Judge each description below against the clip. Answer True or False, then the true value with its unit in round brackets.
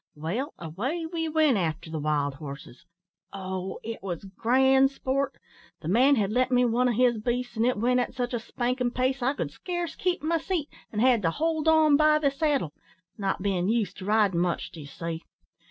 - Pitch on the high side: True (245 Hz)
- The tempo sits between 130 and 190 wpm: False (200 wpm)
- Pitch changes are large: True (6.7 semitones)